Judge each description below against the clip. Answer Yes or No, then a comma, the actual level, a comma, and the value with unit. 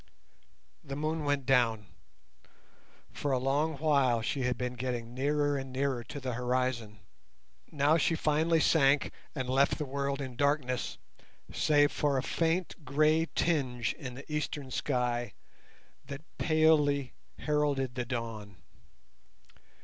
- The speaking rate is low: Yes, slow, 130 wpm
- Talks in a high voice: No, medium, 140 Hz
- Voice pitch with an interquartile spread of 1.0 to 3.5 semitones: Yes, average, 3.0 semitones